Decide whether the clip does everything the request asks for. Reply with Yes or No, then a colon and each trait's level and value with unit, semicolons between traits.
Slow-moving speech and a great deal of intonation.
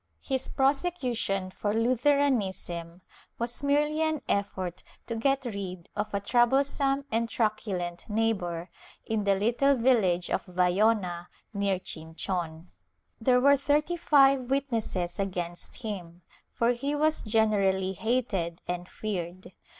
Yes: slow, 120 wpm; wide, 6.4 semitones